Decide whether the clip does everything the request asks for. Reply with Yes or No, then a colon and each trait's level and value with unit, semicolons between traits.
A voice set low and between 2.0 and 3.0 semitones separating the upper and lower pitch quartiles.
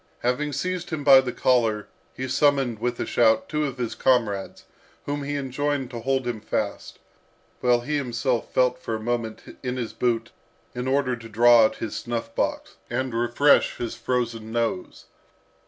Yes: low, 125 Hz; narrow, 2.5 semitones